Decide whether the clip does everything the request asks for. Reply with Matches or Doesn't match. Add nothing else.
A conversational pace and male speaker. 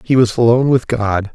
Doesn't match